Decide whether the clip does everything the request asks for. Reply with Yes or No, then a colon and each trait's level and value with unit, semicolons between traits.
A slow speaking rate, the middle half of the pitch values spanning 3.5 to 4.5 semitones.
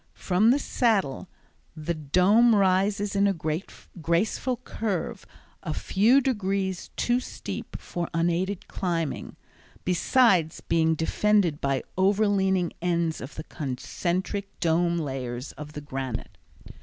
Yes: slow, 115 wpm; average, 4.0 semitones